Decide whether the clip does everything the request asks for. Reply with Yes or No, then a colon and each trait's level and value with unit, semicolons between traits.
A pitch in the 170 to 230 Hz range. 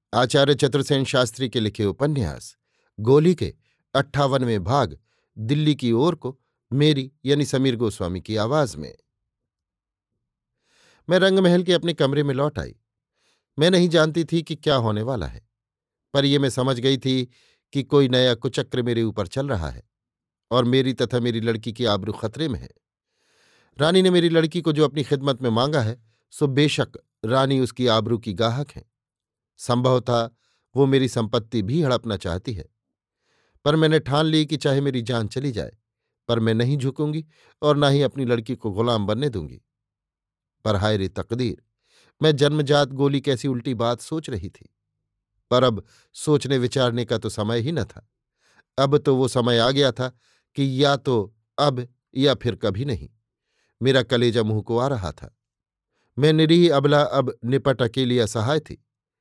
No: low, 130 Hz